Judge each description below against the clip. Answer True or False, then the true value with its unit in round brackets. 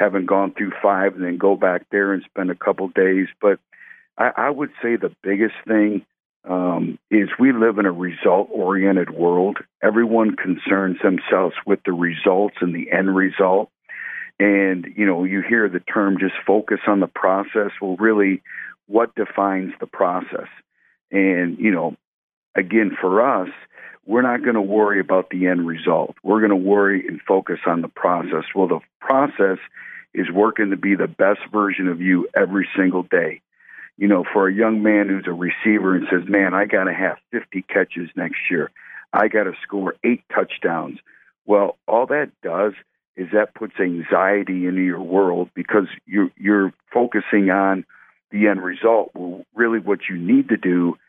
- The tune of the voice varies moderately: False (2.1 semitones)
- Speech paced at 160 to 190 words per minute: True (175 wpm)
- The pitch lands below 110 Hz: True (95 Hz)